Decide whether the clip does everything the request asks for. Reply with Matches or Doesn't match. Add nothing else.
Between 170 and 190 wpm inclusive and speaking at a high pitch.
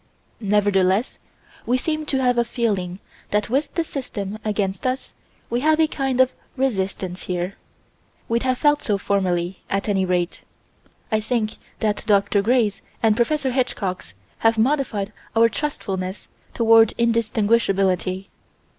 Doesn't match